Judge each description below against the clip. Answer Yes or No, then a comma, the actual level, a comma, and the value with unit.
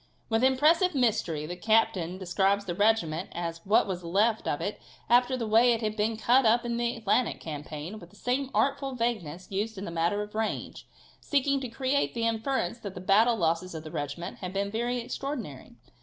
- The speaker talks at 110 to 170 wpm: No, average, 200 wpm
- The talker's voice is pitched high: Yes, high, 215 Hz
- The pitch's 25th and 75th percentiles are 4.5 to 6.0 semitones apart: Yes, average, 5.3 semitones